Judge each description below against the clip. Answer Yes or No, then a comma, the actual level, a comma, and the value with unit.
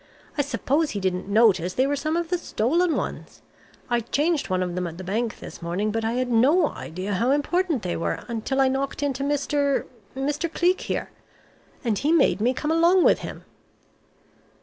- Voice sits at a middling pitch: No, very high, 265 Hz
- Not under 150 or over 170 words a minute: No, average, 195 wpm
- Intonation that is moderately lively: No, wide, 6.1 semitones